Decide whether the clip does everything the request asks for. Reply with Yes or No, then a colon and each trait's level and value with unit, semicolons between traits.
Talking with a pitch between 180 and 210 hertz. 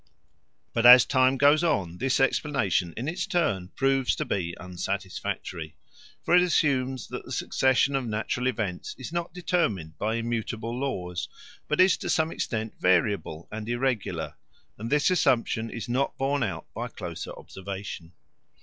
No: low, 120 Hz